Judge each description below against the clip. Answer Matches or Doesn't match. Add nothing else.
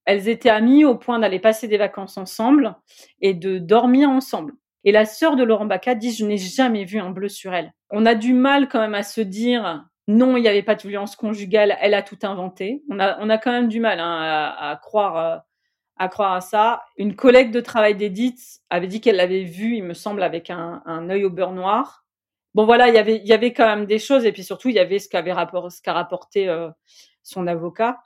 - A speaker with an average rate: Doesn't match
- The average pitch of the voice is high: Matches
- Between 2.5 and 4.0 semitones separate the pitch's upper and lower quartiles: Matches